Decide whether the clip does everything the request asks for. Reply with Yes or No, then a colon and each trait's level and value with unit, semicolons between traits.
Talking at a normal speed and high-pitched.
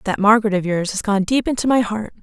No: fast, 270 wpm; high, 215 Hz